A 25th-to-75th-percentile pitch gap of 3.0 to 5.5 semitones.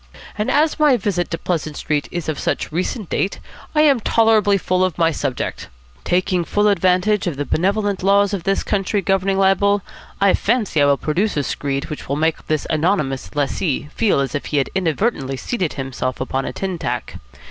Yes: average, 5.1 semitones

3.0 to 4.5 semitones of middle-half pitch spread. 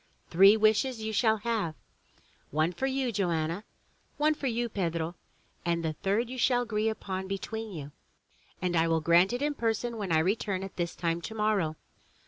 No: average, 5.1 semitones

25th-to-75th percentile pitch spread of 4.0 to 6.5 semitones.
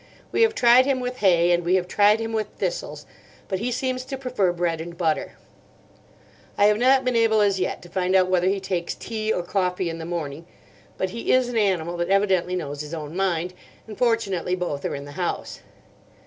Yes: average, 4.7 semitones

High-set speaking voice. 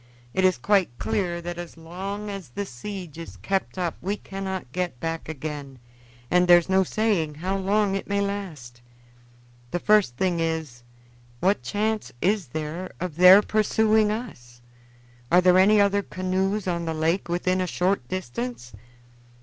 No: medium, 180 Hz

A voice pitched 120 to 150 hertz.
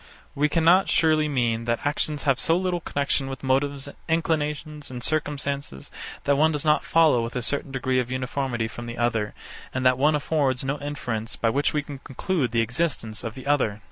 Yes: medium, 140 Hz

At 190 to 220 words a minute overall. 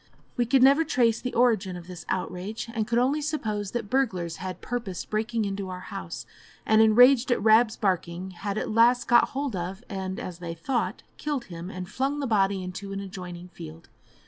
Yes: average, 195 wpm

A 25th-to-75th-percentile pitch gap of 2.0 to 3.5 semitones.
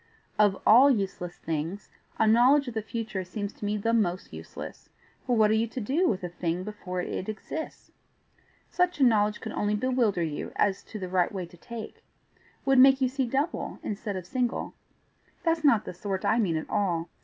No: average, 4.8 semitones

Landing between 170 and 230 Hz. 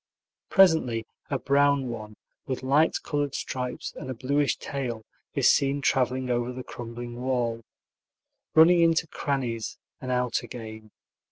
No: low, 130 Hz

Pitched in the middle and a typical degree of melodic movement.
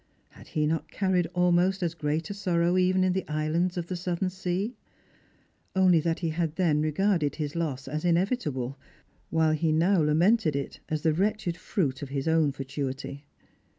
Yes: medium, 165 Hz; average, 3.3 semitones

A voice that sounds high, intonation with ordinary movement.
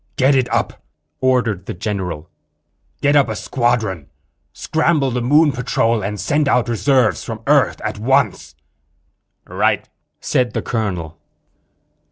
No: low, 120 Hz; average, 4.3 semitones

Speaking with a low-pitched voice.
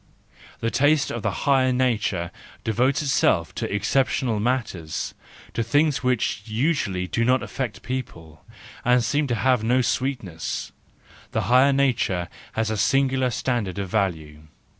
Yes: low, 120 Hz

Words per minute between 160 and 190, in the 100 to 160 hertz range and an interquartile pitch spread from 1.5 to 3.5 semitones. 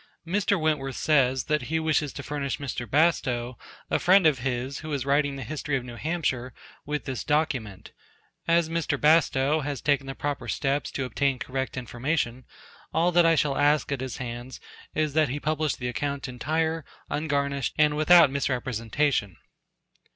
Yes: average, 165 wpm; medium, 140 Hz; average, 3.1 semitones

